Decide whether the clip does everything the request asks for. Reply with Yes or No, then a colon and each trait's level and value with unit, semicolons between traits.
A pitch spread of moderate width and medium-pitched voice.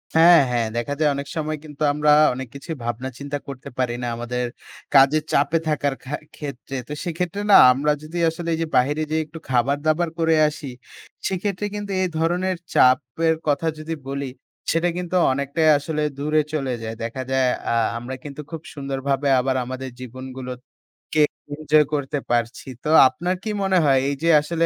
Yes: average, 3.6 semitones; medium, 145 Hz